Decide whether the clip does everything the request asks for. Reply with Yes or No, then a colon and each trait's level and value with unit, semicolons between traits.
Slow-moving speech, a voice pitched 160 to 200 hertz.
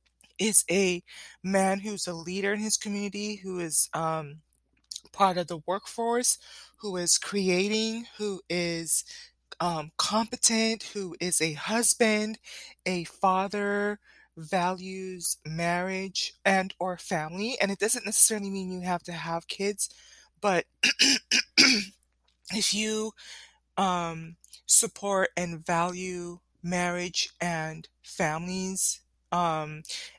Yes: slow, 110 wpm; medium, 185 Hz